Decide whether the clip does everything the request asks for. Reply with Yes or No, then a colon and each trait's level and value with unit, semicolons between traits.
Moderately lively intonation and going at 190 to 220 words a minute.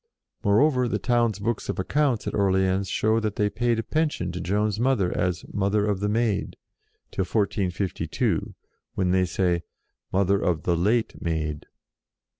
No: average, 3.5 semitones; average, 160 wpm